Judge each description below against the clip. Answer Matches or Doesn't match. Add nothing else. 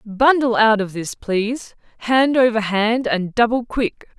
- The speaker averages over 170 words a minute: Doesn't match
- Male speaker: Doesn't match